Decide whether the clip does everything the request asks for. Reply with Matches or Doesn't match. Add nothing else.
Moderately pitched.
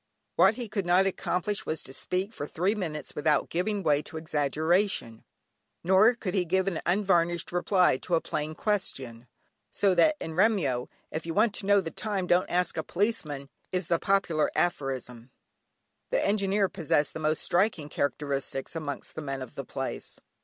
Matches